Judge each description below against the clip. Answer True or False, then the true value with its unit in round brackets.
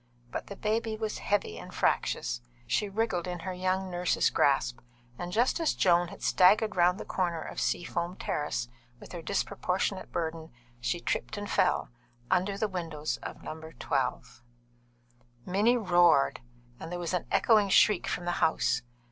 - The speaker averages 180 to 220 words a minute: False (160 wpm)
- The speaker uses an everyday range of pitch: True (3.2 semitones)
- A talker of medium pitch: True (180 Hz)